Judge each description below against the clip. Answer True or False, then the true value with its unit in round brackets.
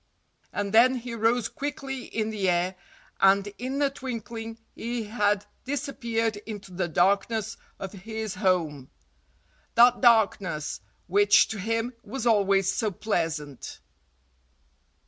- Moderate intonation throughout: True (3.4 semitones)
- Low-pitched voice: False (215 Hz)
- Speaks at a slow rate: True (115 wpm)